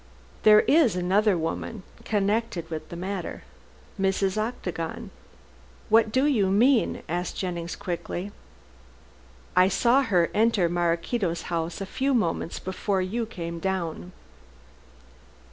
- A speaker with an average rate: No, slow, 115 wpm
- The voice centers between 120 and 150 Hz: No, high, 190 Hz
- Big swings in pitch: No, average, 4.1 semitones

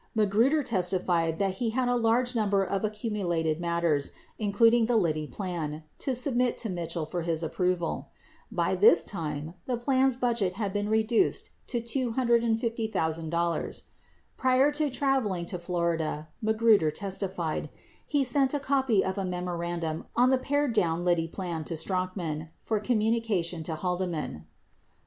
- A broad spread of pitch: Yes, wide, 5.7 semitones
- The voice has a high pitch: Yes, high, 195 Hz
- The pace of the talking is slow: No, average, 145 wpm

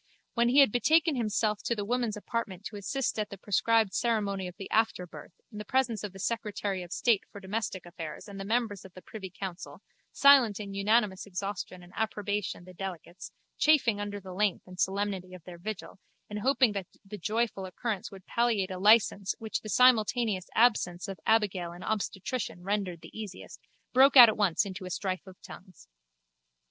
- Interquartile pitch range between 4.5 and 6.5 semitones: No, average, 3.2 semitones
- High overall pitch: Yes, high, 205 Hz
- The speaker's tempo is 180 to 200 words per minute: Yes, average, 185 wpm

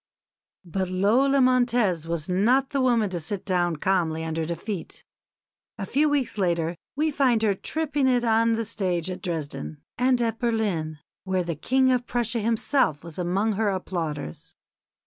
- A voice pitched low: No, high, 205 Hz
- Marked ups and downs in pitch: Yes, wide, 6.1 semitones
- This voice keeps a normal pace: Yes, average, 160 wpm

